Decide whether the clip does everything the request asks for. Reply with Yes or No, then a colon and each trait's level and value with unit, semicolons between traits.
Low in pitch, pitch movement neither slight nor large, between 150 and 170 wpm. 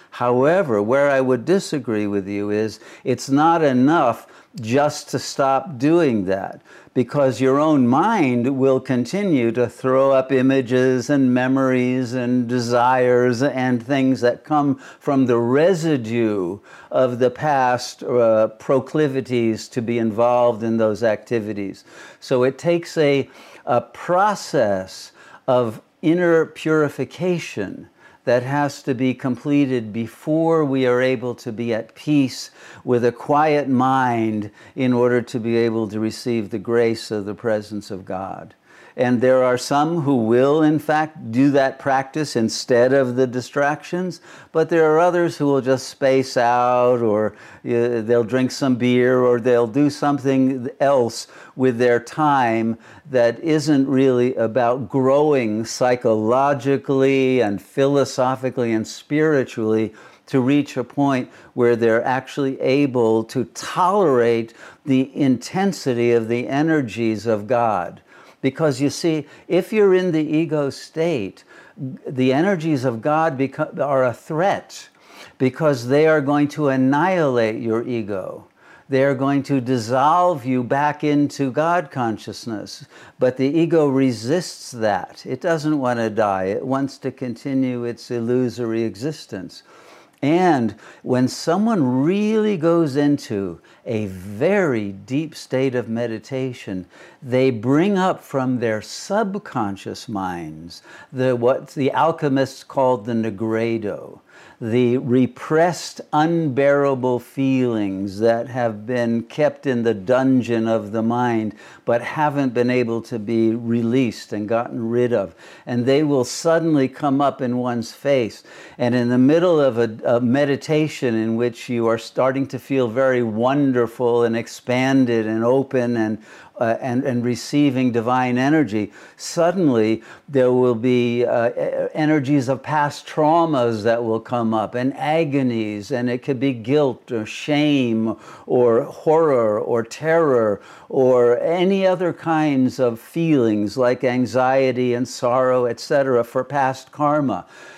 No: low, 130 Hz; average, 3.4 semitones; slow, 135 wpm